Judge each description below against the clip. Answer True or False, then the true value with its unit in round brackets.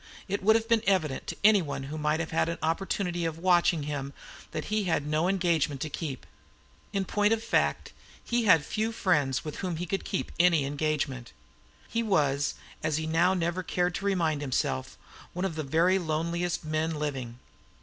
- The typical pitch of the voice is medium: True (165 Hz)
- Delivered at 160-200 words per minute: True (190 wpm)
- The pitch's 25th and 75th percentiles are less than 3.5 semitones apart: False (3.9 semitones)